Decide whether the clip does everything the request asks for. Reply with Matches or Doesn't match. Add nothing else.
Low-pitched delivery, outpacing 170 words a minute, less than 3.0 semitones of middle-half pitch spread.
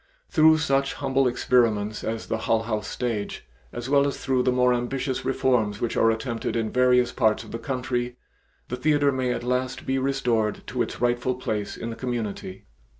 Matches